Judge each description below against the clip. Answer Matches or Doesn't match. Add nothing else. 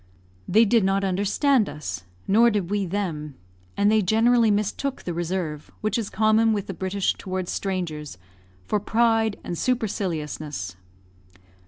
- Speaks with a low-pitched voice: Doesn't match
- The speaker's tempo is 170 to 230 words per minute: Doesn't match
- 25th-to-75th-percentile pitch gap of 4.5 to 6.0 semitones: Doesn't match